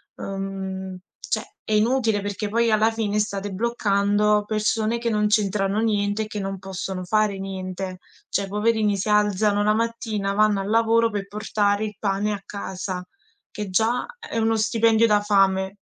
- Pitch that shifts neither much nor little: No, narrow, 1.9 semitones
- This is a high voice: Yes, high, 210 Hz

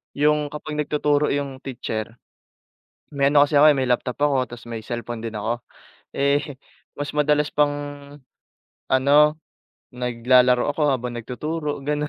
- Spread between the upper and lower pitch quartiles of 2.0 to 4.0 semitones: Yes, average, 3.2 semitones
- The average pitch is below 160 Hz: Yes, medium, 140 Hz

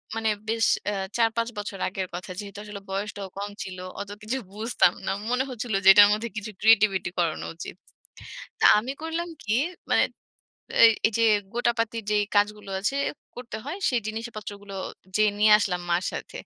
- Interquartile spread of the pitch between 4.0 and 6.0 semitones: No, narrow, 2.4 semitones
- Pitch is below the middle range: No, high, 210 Hz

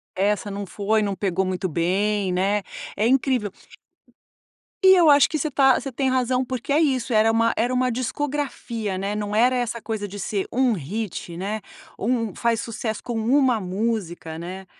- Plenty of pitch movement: No, average, 4.3 semitones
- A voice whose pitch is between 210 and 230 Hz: Yes, high, 220 Hz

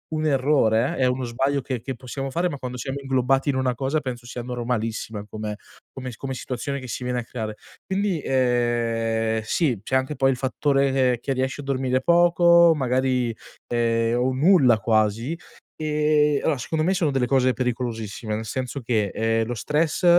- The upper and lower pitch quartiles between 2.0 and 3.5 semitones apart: Yes, average, 2.9 semitones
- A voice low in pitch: Yes, low, 130 Hz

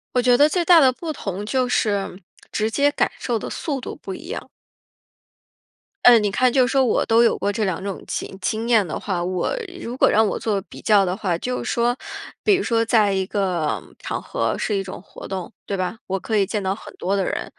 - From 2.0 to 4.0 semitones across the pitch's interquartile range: No, average, 4.4 semitones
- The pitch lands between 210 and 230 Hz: Yes, high, 215 Hz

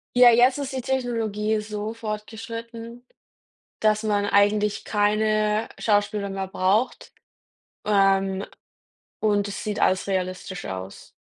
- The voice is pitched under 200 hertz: No, high, 210 Hz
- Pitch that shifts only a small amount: Yes, narrow, 2.1 semitones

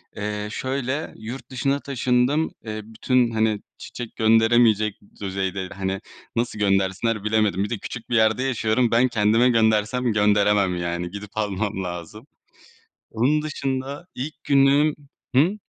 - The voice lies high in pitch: No, low, 110 Hz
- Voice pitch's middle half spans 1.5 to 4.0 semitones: Yes, average, 3.7 semitones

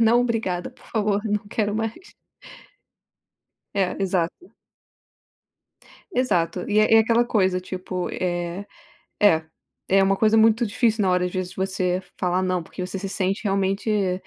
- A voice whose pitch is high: Yes, high, 195 Hz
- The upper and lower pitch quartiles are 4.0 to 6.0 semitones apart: No, average, 3.0 semitones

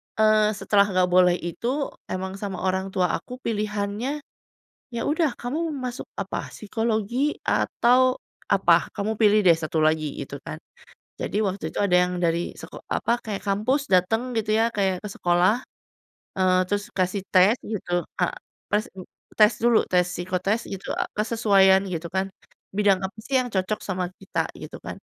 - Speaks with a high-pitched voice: Yes, high, 205 Hz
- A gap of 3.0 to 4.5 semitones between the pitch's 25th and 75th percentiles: Yes, average, 3.6 semitones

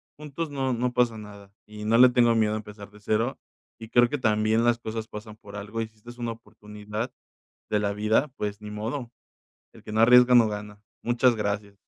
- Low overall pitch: Yes, low, 110 Hz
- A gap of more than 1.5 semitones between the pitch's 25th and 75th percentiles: Yes, narrow, 2.4 semitones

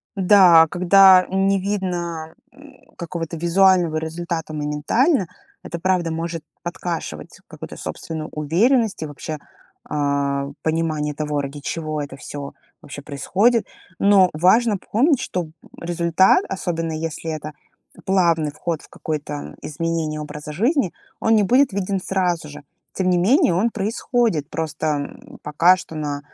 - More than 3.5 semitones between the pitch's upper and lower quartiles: Yes, average, 3.9 semitones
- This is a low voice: No, medium, 170 Hz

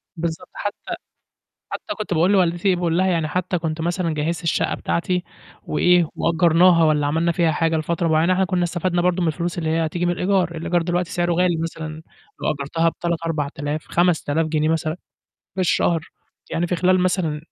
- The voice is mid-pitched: Yes, medium, 170 Hz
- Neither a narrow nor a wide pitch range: No, narrow, 1.9 semitones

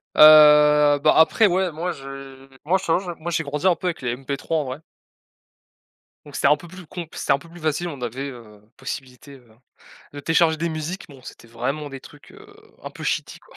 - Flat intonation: No, average, 3.4 semitones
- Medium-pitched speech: Yes, medium, 150 Hz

